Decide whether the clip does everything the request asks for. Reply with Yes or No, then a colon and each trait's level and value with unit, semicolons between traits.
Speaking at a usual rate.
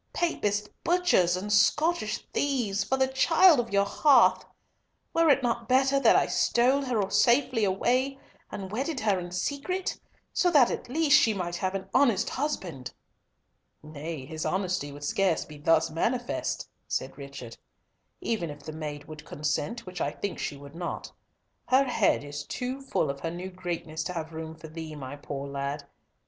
Yes: average, 170 wpm